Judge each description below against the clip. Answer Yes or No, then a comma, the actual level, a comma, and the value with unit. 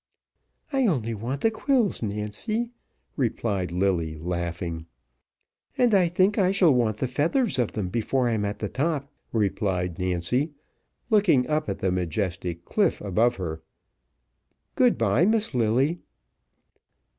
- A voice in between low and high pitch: No, low, 115 Hz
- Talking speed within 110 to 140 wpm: Yes, slow, 135 wpm